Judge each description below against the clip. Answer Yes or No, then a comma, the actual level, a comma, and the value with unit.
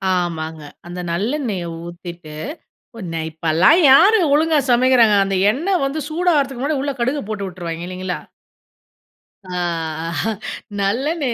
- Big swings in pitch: Yes, wide, 8.5 semitones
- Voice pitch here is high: Yes, high, 215 Hz